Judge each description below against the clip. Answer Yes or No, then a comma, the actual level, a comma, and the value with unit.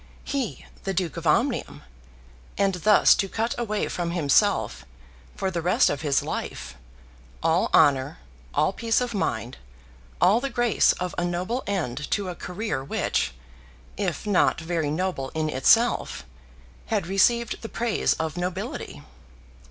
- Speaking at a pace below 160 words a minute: Yes, average, 145 wpm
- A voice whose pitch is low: No, medium, 180 Hz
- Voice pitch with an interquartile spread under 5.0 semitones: No, average, 5.3 semitones